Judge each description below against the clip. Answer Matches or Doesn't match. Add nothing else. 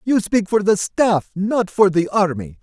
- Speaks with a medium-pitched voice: Doesn't match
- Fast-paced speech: Doesn't match